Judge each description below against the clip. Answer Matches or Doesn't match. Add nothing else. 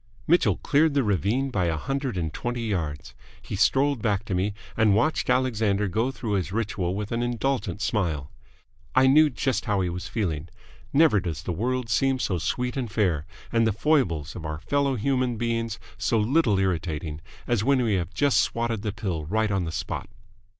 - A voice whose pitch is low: Matches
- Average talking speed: Matches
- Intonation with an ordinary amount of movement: Doesn't match